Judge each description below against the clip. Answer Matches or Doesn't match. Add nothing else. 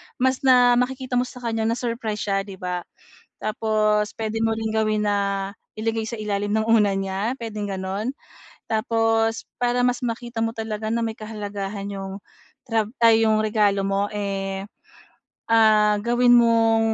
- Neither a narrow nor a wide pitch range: Doesn't match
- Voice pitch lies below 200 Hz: Doesn't match